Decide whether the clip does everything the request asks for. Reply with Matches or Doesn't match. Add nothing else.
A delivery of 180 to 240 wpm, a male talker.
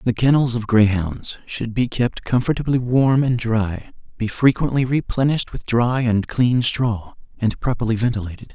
Doesn't match